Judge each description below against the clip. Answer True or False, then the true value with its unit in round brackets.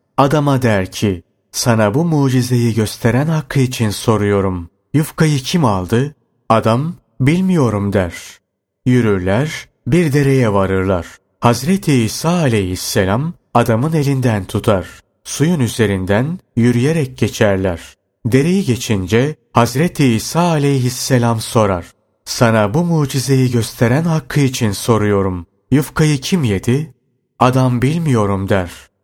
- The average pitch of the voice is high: False (120 Hz)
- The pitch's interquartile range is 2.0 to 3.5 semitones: False (5.4 semitones)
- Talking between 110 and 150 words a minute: False (100 wpm)